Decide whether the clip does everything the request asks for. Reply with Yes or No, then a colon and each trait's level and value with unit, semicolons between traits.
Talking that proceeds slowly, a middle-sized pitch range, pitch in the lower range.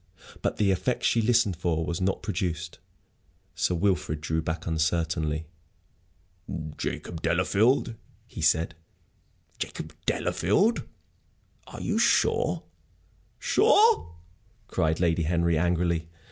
Yes: slow, 105 wpm; average, 3.3 semitones; very low, 85 Hz